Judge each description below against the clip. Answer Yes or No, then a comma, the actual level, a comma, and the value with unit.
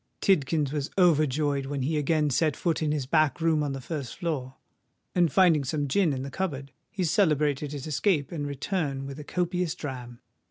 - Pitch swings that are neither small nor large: Yes, average, 3.1 semitones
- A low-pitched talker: No, medium, 150 Hz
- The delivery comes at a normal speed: Yes, average, 190 wpm